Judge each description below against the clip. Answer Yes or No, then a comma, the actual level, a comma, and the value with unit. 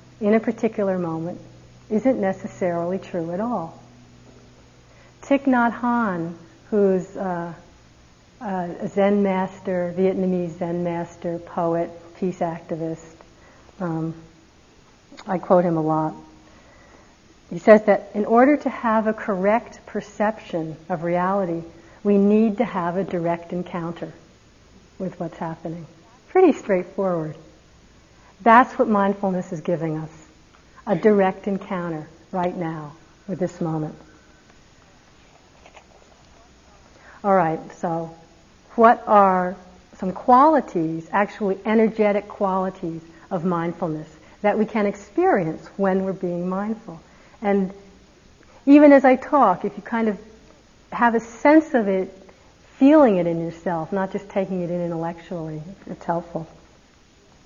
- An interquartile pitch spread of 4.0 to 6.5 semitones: No, average, 3.6 semitones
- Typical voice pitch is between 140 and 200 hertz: Yes, medium, 185 Hz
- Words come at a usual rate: No, slow, 120 wpm